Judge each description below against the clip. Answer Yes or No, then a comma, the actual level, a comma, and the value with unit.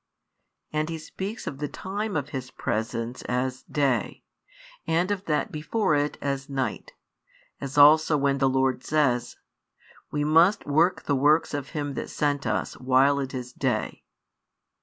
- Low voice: No, medium, 145 Hz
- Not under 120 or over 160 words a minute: Yes, average, 155 wpm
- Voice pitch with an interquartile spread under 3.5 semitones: Yes, average, 2.8 semitones